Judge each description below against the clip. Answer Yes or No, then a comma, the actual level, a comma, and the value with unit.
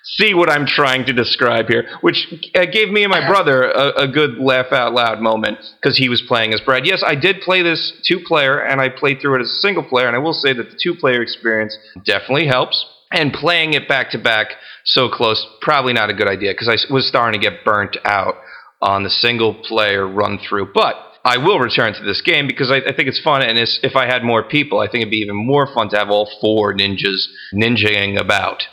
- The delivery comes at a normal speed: No, fast, 240 wpm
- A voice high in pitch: No, low, 125 Hz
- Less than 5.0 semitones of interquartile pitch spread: No, average, 5.3 semitones